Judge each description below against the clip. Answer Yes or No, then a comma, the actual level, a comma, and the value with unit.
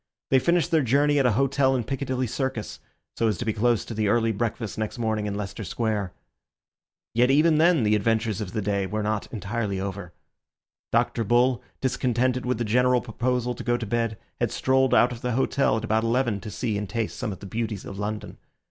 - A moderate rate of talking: No, fast, 210 wpm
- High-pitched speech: No, low, 115 Hz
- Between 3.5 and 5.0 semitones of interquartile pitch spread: No, average, 3.1 semitones